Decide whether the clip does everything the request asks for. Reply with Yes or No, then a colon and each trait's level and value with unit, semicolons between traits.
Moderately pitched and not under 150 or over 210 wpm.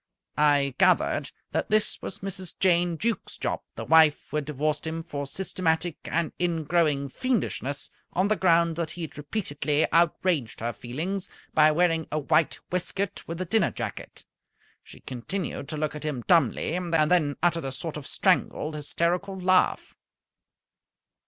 Yes: medium, 165 Hz; average, 155 wpm